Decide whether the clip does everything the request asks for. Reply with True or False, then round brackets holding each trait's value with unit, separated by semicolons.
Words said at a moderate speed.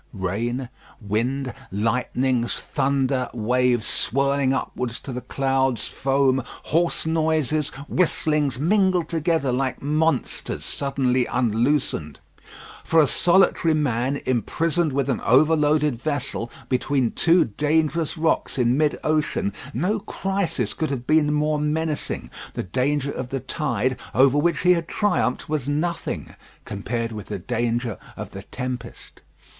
False (125 wpm)